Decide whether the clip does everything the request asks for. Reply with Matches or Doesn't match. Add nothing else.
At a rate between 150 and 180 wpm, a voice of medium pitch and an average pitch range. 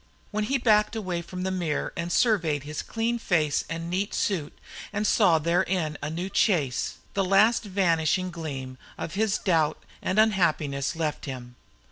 Matches